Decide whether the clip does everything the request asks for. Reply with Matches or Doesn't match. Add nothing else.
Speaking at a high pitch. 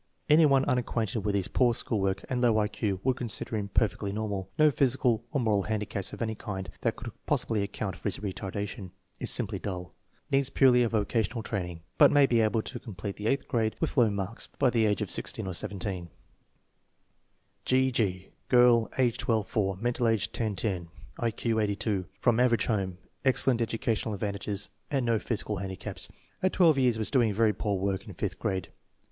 Doesn't match